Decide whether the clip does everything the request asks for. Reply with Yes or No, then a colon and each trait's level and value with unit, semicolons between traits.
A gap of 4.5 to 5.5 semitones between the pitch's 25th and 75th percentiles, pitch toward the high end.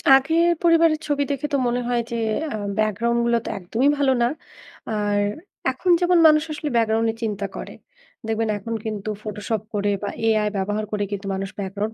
Yes: average, 5.1 semitones; high, 225 Hz